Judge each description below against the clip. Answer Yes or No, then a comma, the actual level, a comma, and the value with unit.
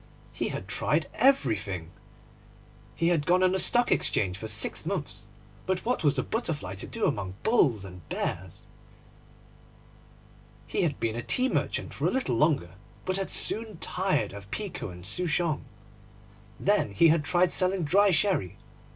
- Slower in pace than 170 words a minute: Yes, average, 160 wpm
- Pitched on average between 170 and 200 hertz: No, medium, 155 Hz